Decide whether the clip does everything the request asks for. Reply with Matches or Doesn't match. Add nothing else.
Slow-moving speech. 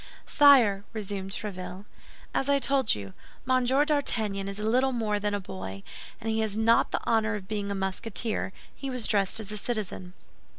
Doesn't match